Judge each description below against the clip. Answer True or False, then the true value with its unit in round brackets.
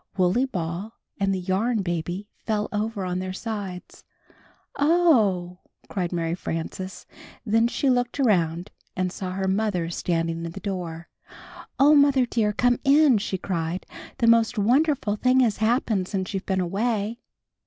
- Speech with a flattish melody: False (4.5 semitones)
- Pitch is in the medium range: False (200 Hz)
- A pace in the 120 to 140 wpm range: False (150 wpm)